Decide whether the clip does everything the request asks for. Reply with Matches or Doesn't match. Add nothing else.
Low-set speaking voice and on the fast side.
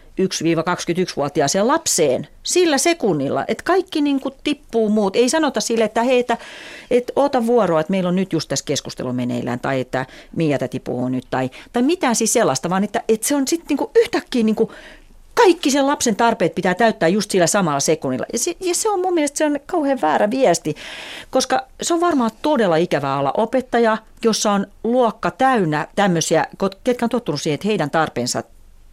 Doesn't match